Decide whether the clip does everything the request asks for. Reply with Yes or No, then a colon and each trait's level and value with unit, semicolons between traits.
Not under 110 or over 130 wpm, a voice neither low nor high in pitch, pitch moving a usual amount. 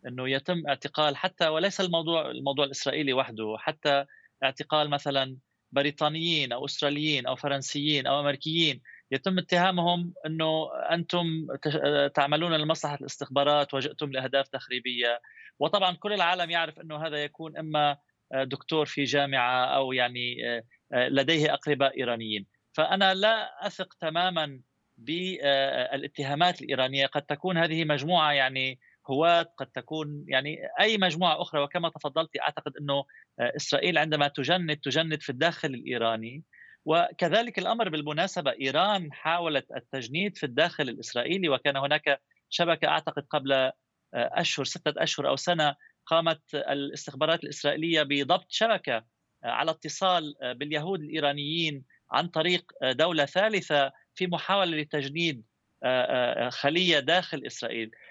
Yes: average, 115 wpm; medium, 150 Hz; average, 3.1 semitones